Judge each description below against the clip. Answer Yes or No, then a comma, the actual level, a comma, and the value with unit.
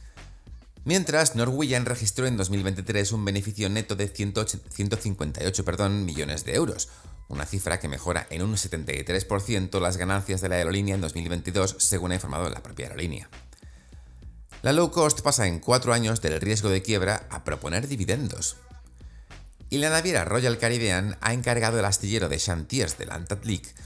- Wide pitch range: No, average, 4.8 semitones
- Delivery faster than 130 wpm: Yes, average, 160 wpm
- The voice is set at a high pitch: No, very low, 95 Hz